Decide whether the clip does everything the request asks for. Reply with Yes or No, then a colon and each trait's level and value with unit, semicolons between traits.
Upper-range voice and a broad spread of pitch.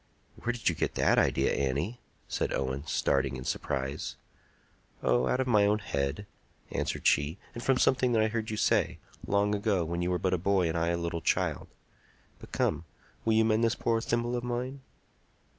No: low, 100 Hz; wide, 6.4 semitones